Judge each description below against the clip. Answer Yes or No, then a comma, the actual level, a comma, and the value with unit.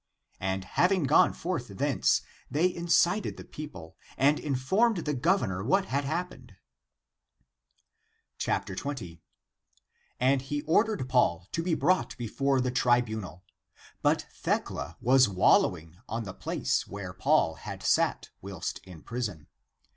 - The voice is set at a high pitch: No, low, 130 Hz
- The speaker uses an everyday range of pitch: No, wide, 8.6 semitones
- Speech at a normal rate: No, slow, 125 wpm